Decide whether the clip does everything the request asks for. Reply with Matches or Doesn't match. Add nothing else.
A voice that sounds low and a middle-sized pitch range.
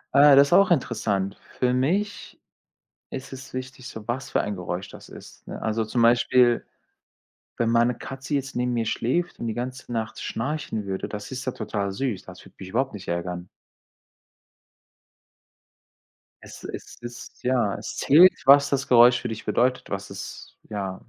Matches